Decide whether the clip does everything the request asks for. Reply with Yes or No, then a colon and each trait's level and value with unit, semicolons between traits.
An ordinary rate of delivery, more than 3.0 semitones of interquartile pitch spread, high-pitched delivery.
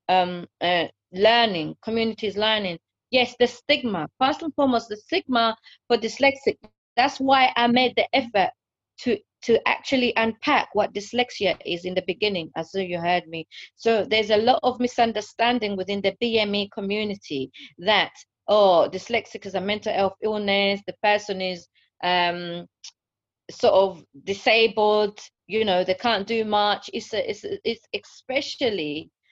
Yes: average, 150 wpm; average, 4.0 semitones; high, 210 Hz